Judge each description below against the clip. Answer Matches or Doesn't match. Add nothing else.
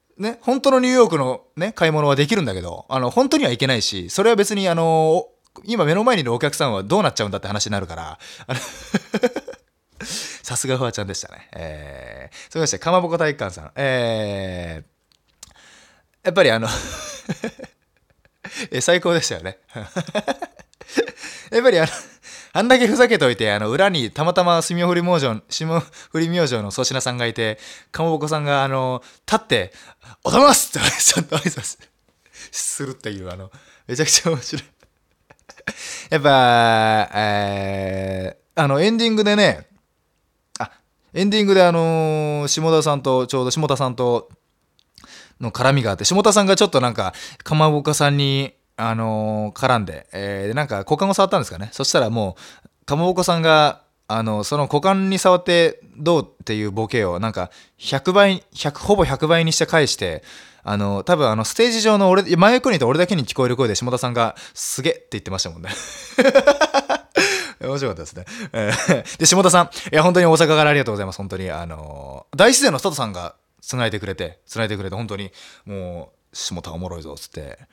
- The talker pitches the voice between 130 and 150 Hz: Matches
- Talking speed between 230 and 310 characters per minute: Doesn't match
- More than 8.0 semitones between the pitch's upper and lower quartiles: Matches